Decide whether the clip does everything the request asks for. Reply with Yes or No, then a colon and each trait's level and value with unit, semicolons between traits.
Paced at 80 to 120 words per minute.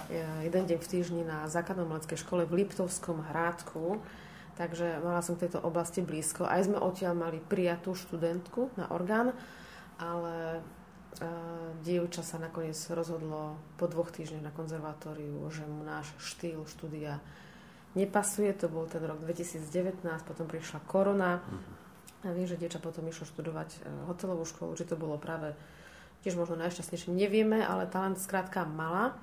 No: average, 145 wpm